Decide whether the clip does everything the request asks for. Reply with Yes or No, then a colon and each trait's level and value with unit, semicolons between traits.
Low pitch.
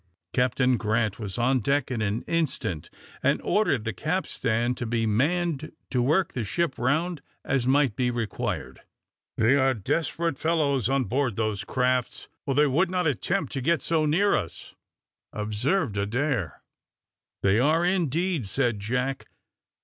Yes: low, 130 Hz